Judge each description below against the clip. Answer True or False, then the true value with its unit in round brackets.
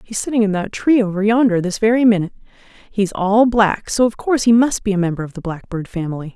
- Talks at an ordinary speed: False (235 wpm)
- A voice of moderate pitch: False (205 Hz)